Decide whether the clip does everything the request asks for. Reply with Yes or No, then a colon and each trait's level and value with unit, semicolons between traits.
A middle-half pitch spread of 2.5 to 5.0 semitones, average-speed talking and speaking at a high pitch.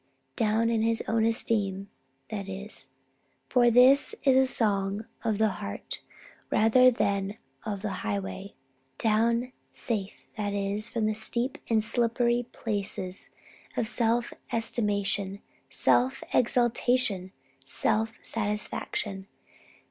No: average, 2.9 semitones; slow, 110 wpm; high, 220 Hz